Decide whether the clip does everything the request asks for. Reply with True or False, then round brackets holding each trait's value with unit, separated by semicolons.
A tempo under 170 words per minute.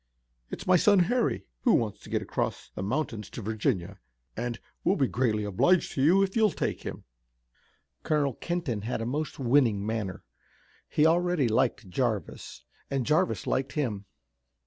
True (160 wpm)